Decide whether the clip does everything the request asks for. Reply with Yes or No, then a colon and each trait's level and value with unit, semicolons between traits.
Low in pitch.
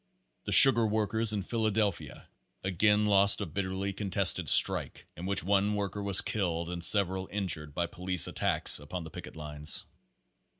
Yes: very low, 95 Hz